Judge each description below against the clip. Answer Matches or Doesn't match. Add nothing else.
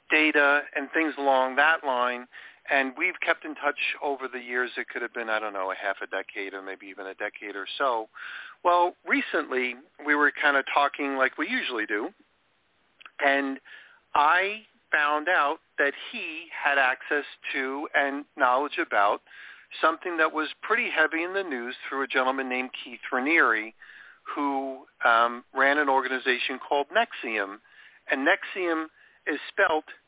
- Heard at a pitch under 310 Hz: Matches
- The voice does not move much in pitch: Doesn't match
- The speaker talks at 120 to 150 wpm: Doesn't match